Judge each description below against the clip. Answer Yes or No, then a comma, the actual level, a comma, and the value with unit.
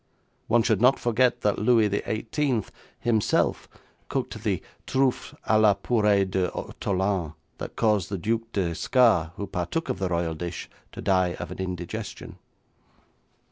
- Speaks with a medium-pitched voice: No, low, 100 Hz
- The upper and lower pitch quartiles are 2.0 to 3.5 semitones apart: No, average, 4.0 semitones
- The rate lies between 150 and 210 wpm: No, average, 140 wpm